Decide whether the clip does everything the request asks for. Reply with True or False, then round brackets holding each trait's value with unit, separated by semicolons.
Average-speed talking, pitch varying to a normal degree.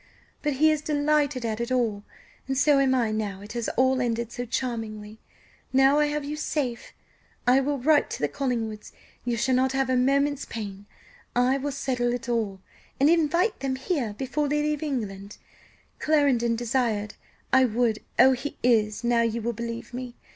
True (180 wpm; 3.4 semitones)